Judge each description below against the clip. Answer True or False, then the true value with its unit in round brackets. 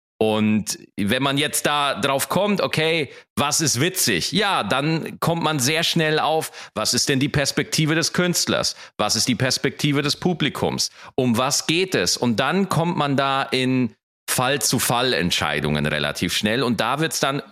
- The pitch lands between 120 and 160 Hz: True (140 Hz)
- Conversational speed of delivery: True (170 wpm)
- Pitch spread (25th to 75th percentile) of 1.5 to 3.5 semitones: False (4.8 semitones)